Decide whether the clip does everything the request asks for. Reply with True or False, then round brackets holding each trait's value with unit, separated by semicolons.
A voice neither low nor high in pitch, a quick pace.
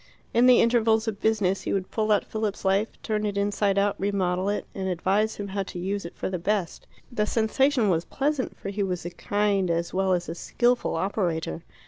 False (200 Hz; 210 wpm)